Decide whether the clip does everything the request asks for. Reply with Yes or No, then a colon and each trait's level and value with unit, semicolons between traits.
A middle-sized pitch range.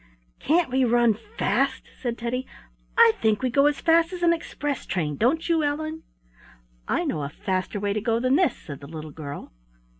No: wide, 7.6 semitones